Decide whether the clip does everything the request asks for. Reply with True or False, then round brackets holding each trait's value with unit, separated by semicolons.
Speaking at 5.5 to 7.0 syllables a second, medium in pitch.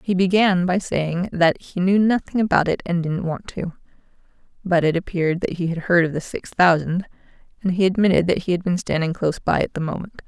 True (5.6 syllables/s; 180 Hz)